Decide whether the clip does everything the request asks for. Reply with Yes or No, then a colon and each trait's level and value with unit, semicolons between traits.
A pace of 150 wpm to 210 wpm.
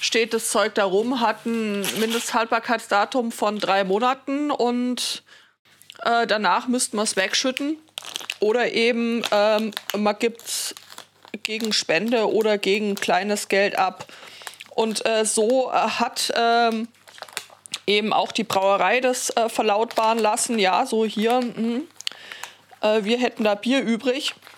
No: average, 130 wpm